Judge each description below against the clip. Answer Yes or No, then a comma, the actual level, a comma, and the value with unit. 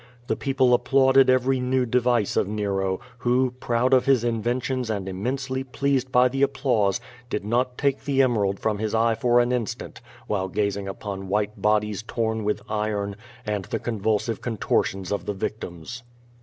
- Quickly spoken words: No, average, 170 wpm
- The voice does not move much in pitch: No, average, 3.6 semitones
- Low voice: Yes, low, 115 Hz